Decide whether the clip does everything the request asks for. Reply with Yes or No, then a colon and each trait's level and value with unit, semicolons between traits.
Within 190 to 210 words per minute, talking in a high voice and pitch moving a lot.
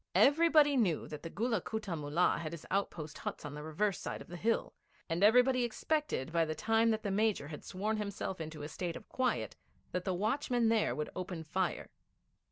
Yes: average, 200 wpm; high, 195 Hz; wide, 5.7 semitones